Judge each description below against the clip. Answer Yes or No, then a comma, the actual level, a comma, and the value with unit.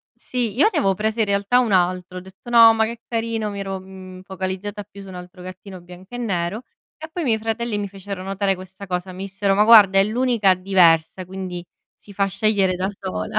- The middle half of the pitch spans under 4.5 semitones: Yes, average, 2.8 semitones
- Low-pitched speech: No, high, 195 Hz